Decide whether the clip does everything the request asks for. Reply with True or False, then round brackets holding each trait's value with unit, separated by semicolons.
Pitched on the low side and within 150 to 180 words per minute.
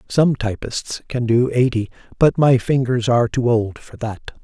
True (120 Hz; 175 wpm)